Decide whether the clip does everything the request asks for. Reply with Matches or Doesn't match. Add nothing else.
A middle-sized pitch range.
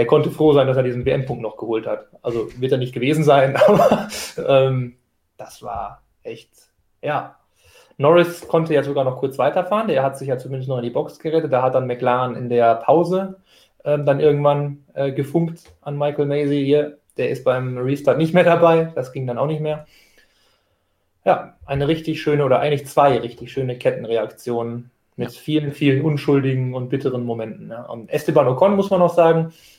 Matches